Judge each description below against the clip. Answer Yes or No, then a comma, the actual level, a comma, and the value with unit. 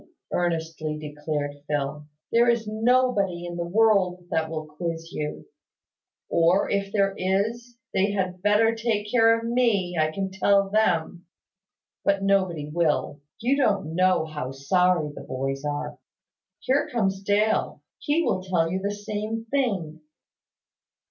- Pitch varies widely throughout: No, average, 5.0 semitones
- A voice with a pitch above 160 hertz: Yes, high, 190 Hz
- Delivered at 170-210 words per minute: No, average, 140 wpm